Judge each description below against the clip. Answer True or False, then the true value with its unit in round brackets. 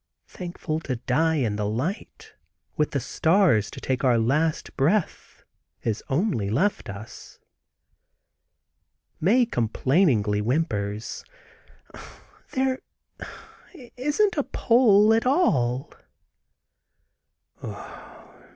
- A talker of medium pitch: True (155 Hz)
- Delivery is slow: True (85 wpm)